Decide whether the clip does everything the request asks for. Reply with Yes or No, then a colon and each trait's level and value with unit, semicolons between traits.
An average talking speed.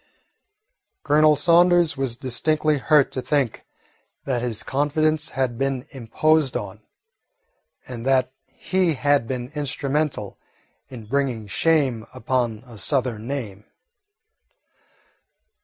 No: slow, 105 wpm